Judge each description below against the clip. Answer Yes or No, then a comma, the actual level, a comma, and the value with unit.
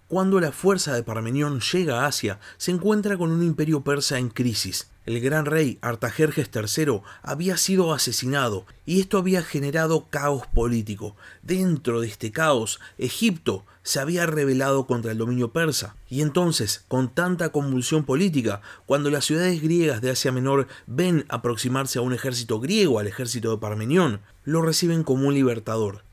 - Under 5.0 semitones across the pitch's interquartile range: No, wide, 5.5 semitones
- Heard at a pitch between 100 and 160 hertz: Yes, low, 135 Hz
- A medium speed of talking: Yes, average, 160 wpm